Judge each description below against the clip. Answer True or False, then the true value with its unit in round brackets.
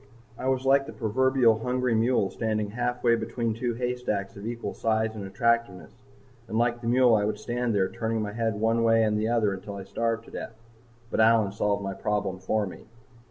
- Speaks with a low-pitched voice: True (115 Hz)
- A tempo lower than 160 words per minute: False (205 wpm)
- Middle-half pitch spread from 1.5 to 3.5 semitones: True (2.4 semitones)